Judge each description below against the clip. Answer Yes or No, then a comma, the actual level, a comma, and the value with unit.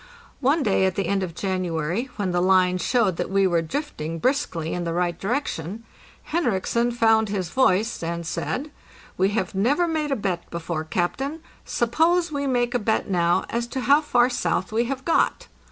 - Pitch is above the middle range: Yes, high, 205 Hz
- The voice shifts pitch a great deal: Yes, wide, 6.6 semitones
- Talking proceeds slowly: No, average, 185 wpm